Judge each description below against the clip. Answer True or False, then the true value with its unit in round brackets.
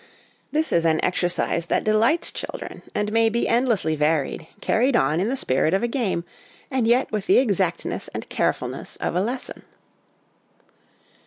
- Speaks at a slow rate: False (160 wpm)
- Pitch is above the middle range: True (210 Hz)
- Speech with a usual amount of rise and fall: False (6.0 semitones)